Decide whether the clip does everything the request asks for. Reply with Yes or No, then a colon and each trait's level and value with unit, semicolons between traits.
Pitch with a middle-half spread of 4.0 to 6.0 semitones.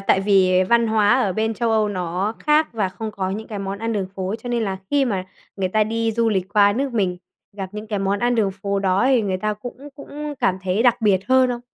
No: average, 3.2 semitones